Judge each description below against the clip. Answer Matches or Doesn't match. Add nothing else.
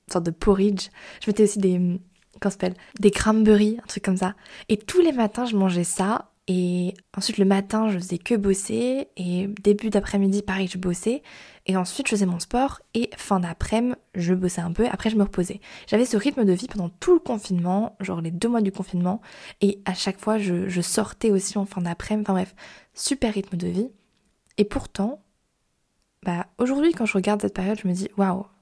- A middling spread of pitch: Matches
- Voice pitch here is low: Doesn't match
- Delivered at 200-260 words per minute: Matches